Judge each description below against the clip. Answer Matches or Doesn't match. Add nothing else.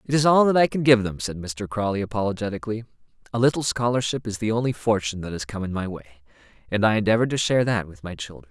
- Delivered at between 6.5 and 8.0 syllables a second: Matches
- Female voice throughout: Doesn't match